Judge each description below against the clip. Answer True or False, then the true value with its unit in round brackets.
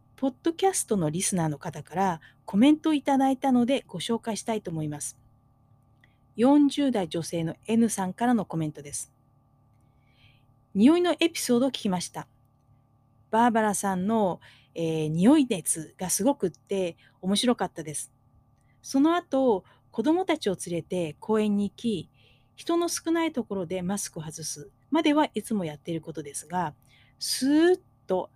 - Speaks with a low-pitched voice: False (185 Hz)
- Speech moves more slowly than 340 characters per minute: True (305 characters per minute)